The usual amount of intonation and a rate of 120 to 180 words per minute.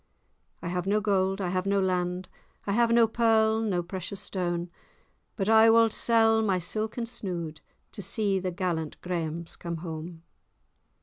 Yes: average, 3.8 semitones; average, 160 wpm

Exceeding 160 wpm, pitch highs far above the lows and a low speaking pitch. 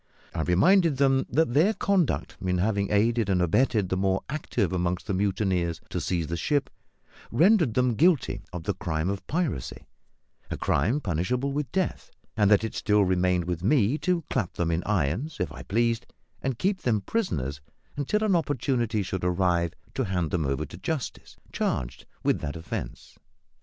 Yes: average, 175 wpm; wide, 7.7 semitones; low, 105 Hz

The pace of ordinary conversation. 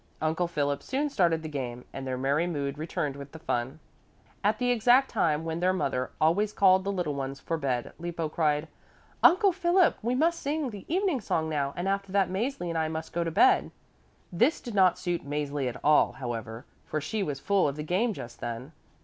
No: fast, 210 wpm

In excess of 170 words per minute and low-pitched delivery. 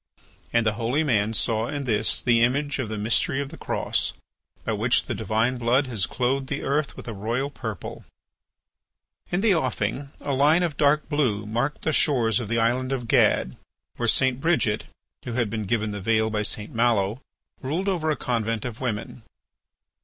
Yes: average, 185 wpm; low, 120 Hz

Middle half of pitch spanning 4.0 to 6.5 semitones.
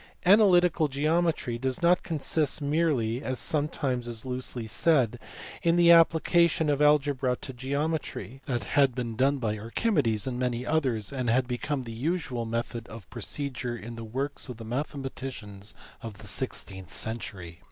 Yes: average, 4.3 semitones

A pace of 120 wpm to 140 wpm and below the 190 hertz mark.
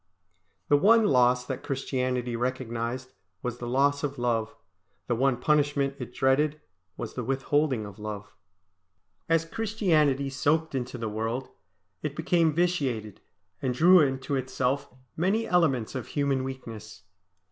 Yes: slow, 135 wpm; low, 135 Hz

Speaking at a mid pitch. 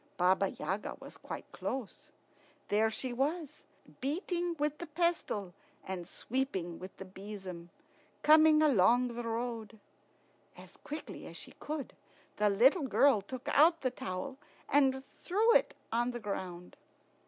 No: high, 245 Hz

